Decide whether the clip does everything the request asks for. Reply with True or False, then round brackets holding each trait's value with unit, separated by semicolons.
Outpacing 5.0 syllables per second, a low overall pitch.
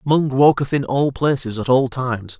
False (4.9 syllables/s; 130 Hz)